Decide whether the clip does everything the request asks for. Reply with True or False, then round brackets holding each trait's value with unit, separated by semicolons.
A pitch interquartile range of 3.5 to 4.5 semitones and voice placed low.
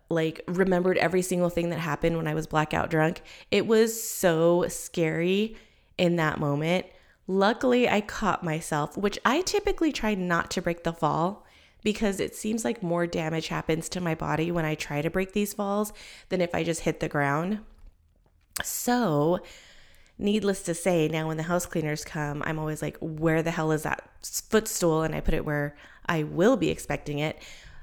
False (4.0 semitones; 170 Hz)